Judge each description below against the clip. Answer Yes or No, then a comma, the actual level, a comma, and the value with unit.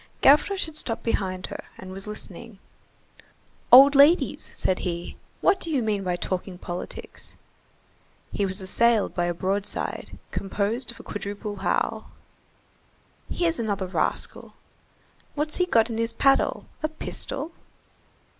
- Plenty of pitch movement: Yes, wide, 6.4 semitones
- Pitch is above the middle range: Yes, high, 215 Hz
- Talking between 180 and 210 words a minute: No, slow, 135 wpm